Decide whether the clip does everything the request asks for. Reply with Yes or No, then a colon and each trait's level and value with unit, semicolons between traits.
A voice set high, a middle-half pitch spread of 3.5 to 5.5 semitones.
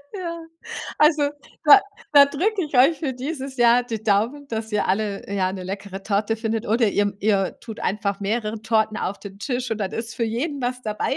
Yes: high, 225 Hz; average, 4.8 semitones